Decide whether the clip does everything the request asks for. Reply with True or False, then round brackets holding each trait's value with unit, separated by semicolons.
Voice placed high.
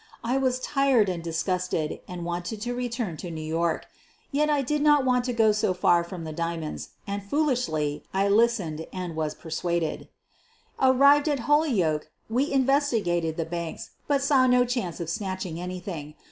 True (195 Hz)